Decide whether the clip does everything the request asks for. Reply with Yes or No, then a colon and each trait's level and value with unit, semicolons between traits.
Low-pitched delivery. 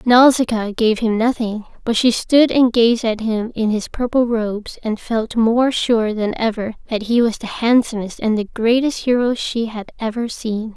No: high, 230 Hz